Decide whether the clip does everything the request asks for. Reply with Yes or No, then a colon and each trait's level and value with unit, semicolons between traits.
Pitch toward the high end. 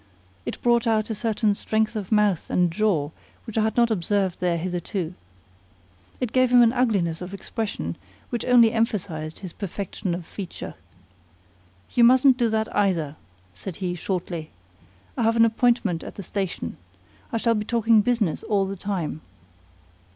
Yes: high, 210 Hz